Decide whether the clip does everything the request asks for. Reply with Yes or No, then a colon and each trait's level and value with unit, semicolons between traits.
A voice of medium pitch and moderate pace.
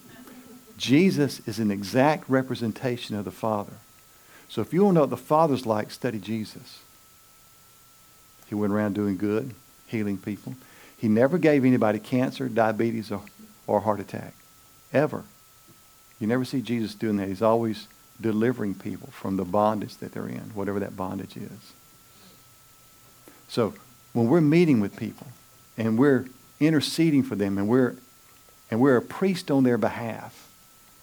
No: low, 120 Hz; average, 150 wpm